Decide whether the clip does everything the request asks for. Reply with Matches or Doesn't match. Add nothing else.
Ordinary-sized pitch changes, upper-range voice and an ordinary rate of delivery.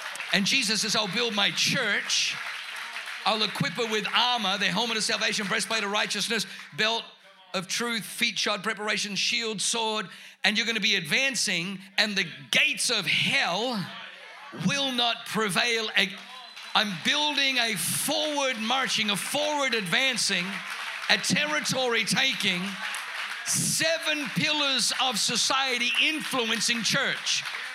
Doesn't match